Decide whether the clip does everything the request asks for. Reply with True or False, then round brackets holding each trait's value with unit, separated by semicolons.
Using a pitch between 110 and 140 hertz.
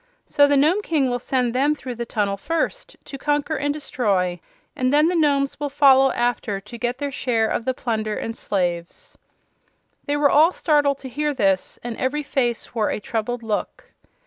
False (260 Hz)